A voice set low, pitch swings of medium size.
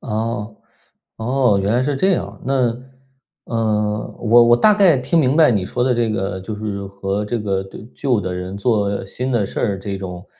Yes: low, 110 Hz; average, 4.0 semitones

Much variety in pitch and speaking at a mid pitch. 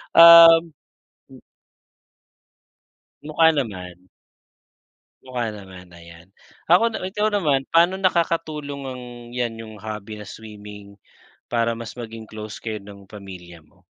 No: wide, 7.5 semitones; low, 115 Hz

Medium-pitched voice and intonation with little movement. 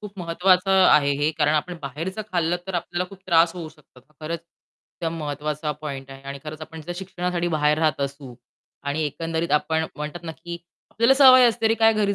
No: medium, 165 Hz; average, 3.2 semitones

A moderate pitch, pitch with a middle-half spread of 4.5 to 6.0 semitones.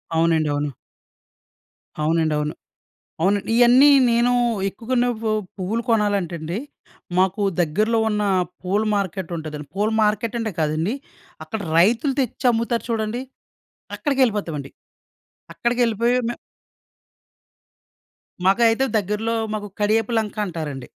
No: high, 210 Hz; average, 5.1 semitones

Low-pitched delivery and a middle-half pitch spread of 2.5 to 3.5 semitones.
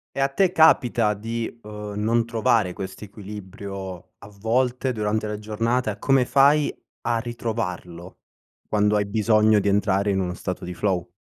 Yes: low, 105 Hz; average, 2.8 semitones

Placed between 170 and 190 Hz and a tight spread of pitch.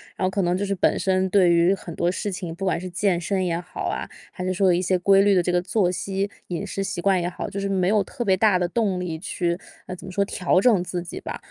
Yes: medium, 185 Hz; narrow, 1.9 semitones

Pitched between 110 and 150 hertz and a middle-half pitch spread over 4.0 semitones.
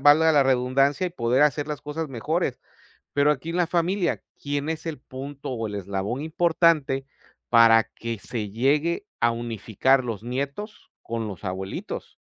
Yes: low, 135 Hz; average, 5.1 semitones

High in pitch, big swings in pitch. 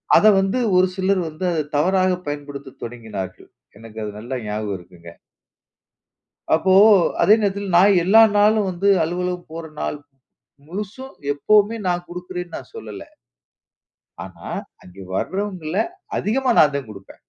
No: medium, 175 Hz; wide, 6.9 semitones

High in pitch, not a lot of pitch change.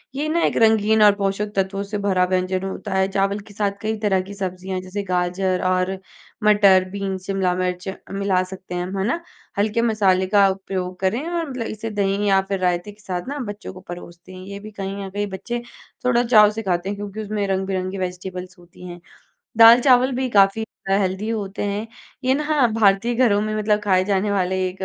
Yes: high, 195 Hz; narrow, 2.2 semitones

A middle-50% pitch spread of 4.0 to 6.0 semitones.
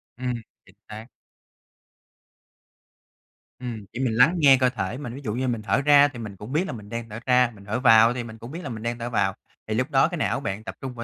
No: average, 3.2 semitones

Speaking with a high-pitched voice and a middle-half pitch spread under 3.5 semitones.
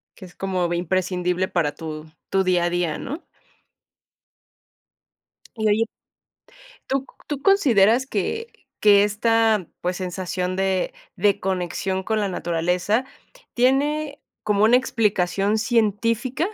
No: high, 200 Hz; average, 4.3 semitones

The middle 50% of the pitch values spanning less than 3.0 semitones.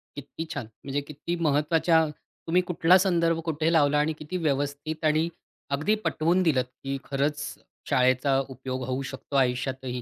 No: average, 3.3 semitones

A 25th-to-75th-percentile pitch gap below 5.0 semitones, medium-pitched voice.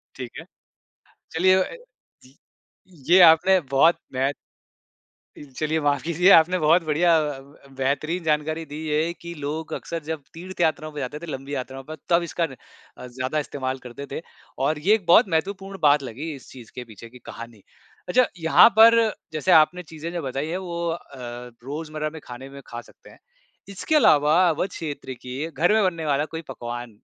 Yes: average, 4.1 semitones; medium, 155 Hz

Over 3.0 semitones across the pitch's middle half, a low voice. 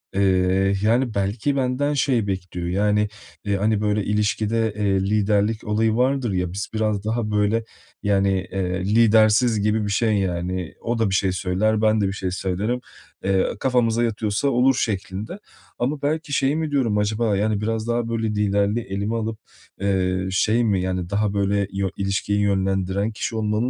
No: narrow, 2.6 semitones; low, 105 Hz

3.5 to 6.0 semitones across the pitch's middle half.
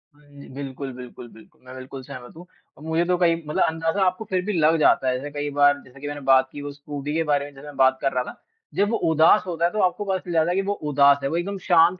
Yes: average, 3.9 semitones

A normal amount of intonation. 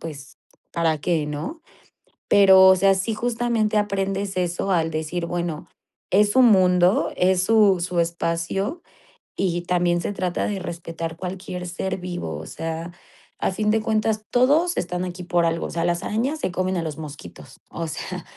Yes: average, 3.2 semitones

